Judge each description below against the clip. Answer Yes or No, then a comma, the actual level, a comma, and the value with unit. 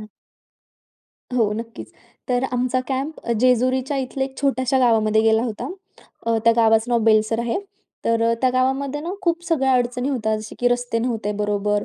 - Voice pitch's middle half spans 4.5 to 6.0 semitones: No, average, 2.8 semitones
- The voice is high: Yes, high, 245 Hz